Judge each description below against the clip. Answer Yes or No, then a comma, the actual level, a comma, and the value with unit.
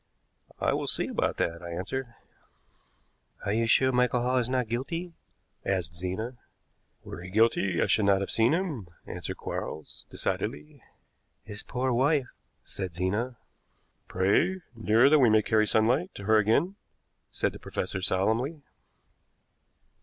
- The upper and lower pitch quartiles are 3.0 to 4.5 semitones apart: No, average, 5.0 semitones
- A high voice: No, low, 115 Hz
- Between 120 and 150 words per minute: Yes, average, 145 wpm